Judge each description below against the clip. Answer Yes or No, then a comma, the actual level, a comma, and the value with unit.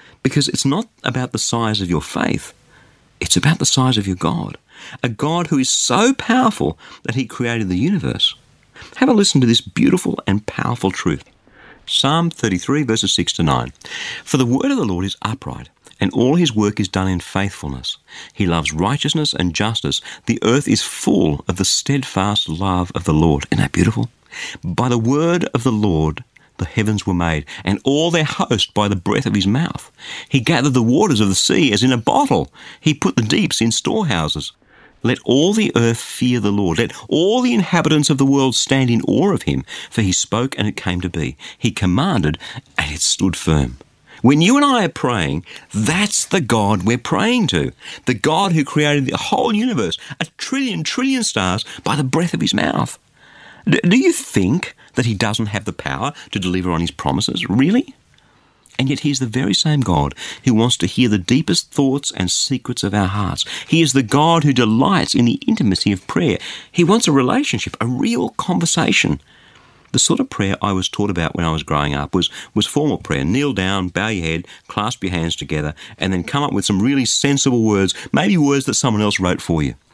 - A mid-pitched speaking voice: No, low, 120 Hz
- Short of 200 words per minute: No, fast, 205 wpm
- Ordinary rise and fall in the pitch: No, wide, 7.5 semitones